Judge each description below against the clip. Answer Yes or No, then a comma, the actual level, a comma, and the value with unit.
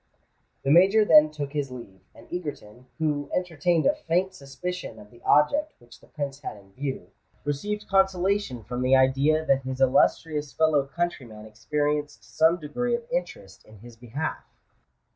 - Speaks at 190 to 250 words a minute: No, average, 150 wpm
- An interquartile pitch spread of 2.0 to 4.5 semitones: No, average, 5.1 semitones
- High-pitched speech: No, medium, 145 Hz